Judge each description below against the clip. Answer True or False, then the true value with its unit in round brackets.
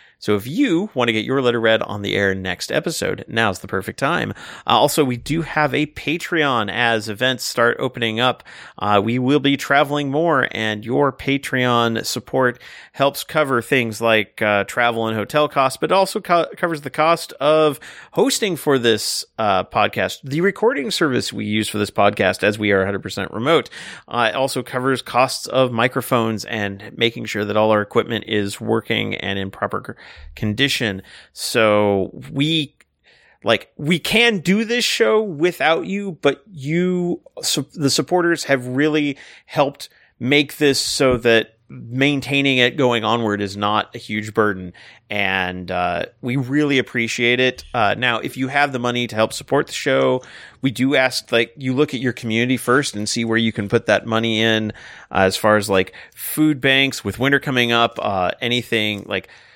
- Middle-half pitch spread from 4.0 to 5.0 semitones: True (4.7 semitones)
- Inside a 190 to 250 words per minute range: False (175 wpm)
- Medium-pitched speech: False (125 Hz)